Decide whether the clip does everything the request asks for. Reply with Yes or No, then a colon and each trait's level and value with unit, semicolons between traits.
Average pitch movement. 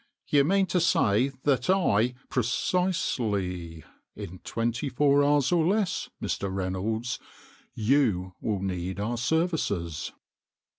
No: wide, 7.2 semitones